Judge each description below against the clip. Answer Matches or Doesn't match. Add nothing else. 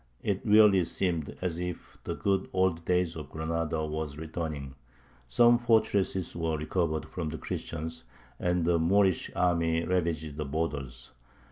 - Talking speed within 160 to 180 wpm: Doesn't match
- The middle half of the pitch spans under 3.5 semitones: Matches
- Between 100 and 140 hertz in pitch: Doesn't match